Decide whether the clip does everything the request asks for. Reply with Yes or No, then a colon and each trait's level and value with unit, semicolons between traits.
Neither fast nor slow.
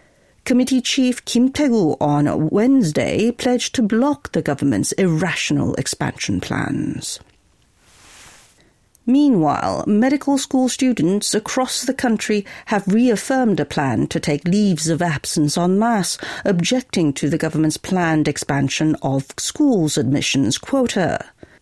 No: slow, 115 wpm